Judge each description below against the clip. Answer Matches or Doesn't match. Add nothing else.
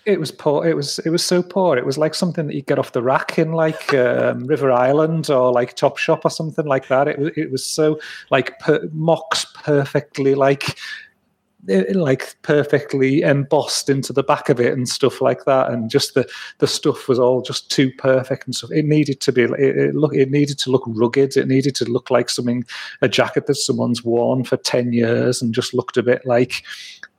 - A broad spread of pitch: Doesn't match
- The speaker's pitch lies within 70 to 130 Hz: Doesn't match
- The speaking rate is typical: Doesn't match